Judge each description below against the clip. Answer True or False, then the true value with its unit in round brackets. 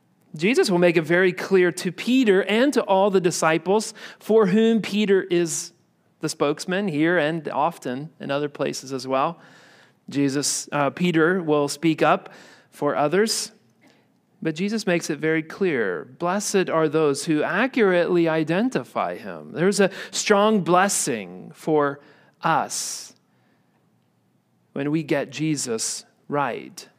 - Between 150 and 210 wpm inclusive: False (135 wpm)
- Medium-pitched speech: True (175 Hz)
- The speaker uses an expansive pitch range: False (4.7 semitones)